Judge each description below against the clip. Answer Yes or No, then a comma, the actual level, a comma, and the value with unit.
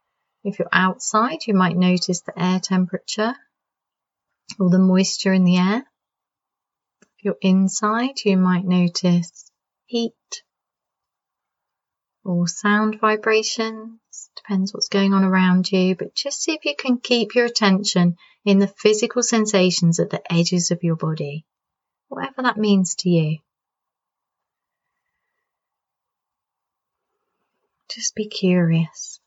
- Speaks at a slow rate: Yes, slow, 120 wpm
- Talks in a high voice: Yes, high, 195 Hz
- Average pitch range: Yes, average, 3.4 semitones